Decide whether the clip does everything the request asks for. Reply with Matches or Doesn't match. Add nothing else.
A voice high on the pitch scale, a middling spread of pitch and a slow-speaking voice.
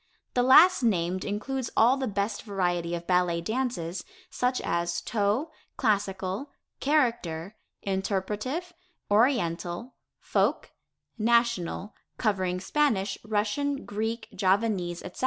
Matches